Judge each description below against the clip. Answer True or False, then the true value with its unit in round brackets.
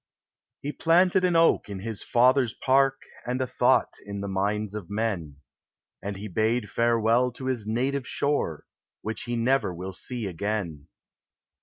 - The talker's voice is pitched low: True (115 Hz)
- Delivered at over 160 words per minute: False (155 wpm)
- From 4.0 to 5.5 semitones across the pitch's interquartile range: True (4.3 semitones)